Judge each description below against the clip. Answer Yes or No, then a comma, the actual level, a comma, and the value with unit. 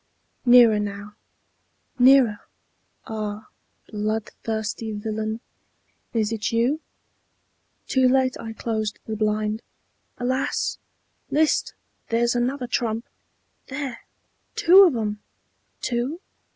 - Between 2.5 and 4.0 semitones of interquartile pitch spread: Yes, average, 2.8 semitones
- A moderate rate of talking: No, slow, 90 wpm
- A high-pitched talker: Yes, high, 225 Hz